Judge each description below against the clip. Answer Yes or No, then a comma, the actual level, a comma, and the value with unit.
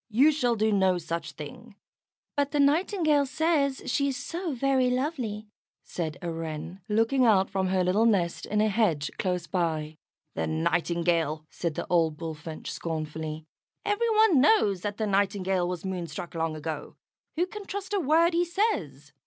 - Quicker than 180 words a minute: No, average, 165 wpm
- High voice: Yes, high, 200 Hz